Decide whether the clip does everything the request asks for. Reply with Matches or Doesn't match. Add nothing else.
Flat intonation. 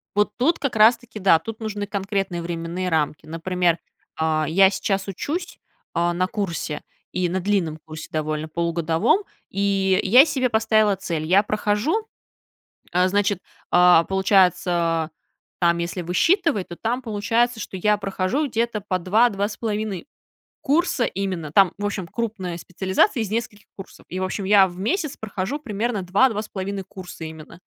Doesn't match